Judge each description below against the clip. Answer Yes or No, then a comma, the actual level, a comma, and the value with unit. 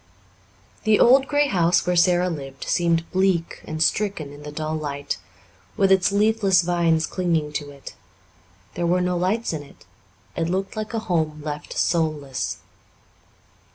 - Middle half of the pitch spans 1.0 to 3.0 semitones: No, average, 3.8 semitones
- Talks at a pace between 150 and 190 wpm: Yes, average, 155 wpm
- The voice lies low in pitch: No, medium, 170 Hz